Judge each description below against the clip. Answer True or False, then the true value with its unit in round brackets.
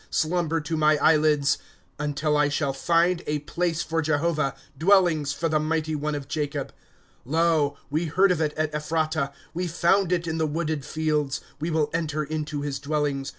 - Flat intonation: True (1.8 semitones)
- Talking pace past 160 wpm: True (195 wpm)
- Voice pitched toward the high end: False (155 Hz)